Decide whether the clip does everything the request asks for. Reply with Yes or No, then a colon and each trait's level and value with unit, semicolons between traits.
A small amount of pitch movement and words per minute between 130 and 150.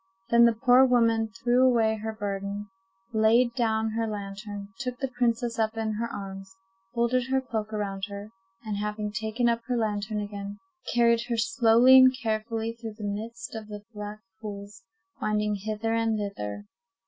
No: narrow, 2.0 semitones; average, 165 wpm